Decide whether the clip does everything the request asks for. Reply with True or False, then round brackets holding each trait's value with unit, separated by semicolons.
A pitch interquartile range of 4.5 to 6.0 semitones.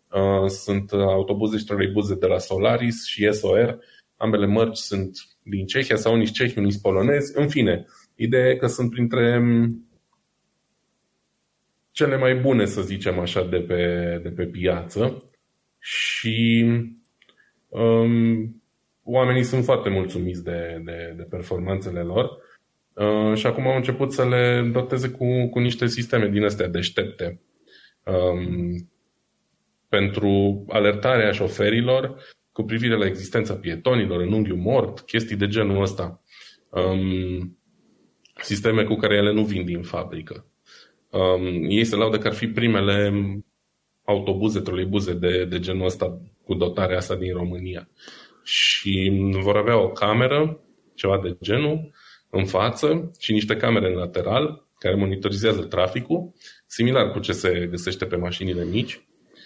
False (4.0 semitones)